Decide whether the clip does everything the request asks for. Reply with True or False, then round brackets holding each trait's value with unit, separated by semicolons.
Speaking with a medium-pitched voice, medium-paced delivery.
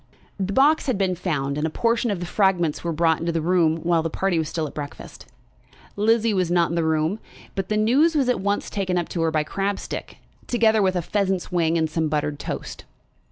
False (180 Hz; 225 wpm)